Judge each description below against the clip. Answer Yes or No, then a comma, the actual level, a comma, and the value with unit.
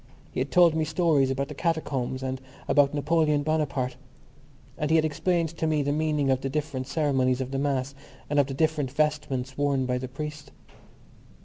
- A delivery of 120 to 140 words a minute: No, average, 190 wpm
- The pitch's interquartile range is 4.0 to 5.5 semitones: No, average, 2.7 semitones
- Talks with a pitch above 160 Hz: No, medium, 145 Hz